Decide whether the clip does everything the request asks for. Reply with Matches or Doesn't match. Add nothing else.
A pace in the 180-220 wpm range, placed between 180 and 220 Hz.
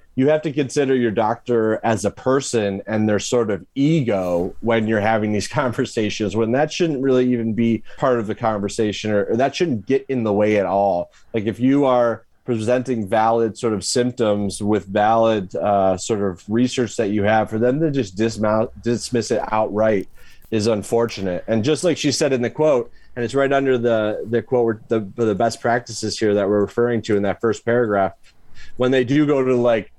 Doesn't match